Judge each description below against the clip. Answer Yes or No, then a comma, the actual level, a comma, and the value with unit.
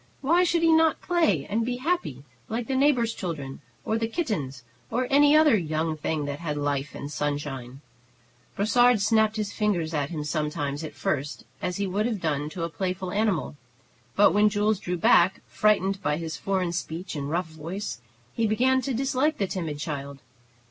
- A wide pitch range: Yes, wide, 7.0 semitones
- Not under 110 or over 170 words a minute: No, average, 185 wpm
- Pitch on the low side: No, medium, 185 Hz